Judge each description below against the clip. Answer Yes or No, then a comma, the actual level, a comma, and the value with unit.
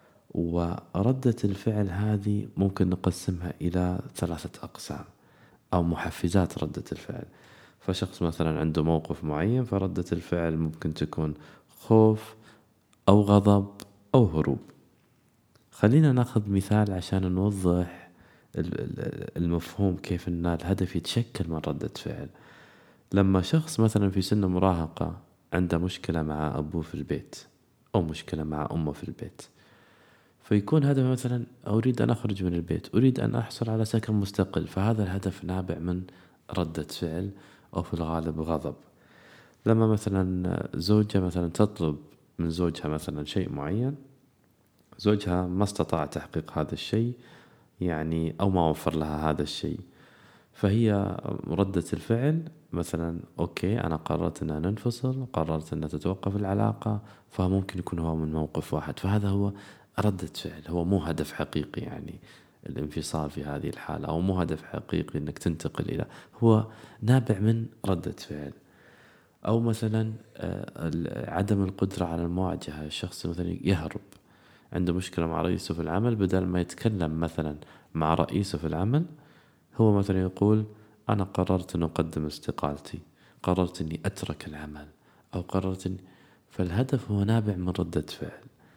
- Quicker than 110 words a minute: Yes, average, 130 wpm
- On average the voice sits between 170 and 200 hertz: No, very low, 95 Hz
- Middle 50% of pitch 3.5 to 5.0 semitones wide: Yes, average, 4.3 semitones